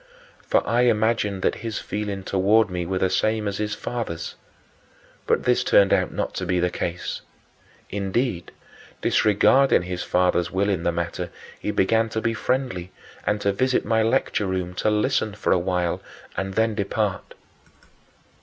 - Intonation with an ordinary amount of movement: Yes, average, 3.3 semitones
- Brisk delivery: No, average, 165 wpm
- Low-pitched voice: Yes, low, 100 Hz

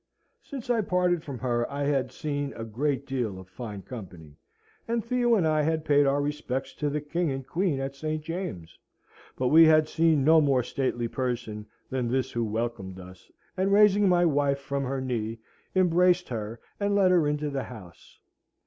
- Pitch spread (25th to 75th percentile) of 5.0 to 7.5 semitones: Yes, average, 5.3 semitones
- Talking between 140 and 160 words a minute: No, average, 185 wpm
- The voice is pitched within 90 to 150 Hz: Yes, medium, 140 Hz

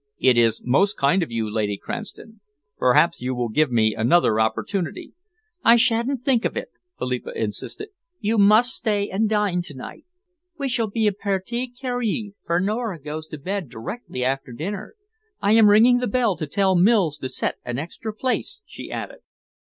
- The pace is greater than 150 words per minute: Yes, average, 175 wpm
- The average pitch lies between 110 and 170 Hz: No, high, 195 Hz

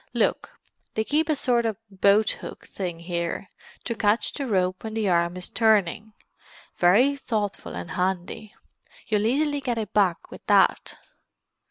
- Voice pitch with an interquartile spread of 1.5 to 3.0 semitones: No, average, 4.2 semitones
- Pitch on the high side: Yes, high, 210 Hz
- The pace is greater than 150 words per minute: No, average, 140 wpm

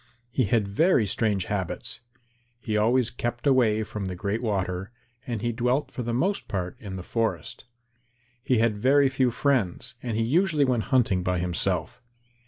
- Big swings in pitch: No, average, 4.2 semitones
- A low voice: Yes, low, 115 Hz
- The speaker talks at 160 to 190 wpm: Yes, average, 170 wpm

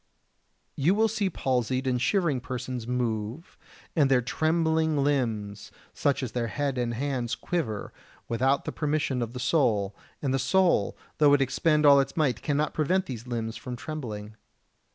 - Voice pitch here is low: Yes, low, 130 Hz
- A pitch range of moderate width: Yes, average, 4.2 semitones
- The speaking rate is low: No, average, 165 wpm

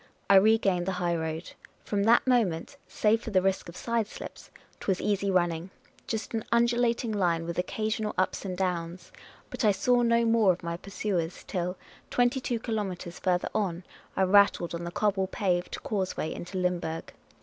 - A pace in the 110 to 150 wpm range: No, average, 175 wpm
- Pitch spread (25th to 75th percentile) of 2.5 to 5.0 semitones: Yes, average, 3.9 semitones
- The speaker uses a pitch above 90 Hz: Yes, high, 190 Hz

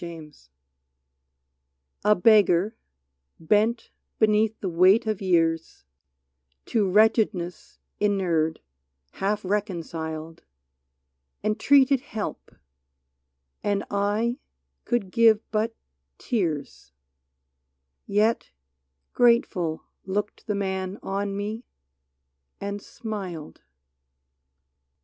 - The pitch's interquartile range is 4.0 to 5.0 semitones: Yes, average, 4.4 semitones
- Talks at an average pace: No, slow, 80 wpm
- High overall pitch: Yes, high, 200 Hz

